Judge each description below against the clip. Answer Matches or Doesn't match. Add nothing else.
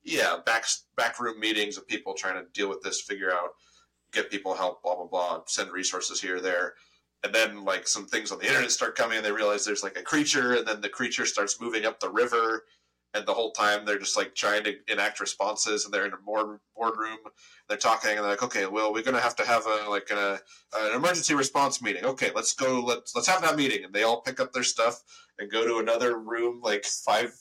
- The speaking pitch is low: Matches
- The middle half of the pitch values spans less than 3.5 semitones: Doesn't match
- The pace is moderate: Doesn't match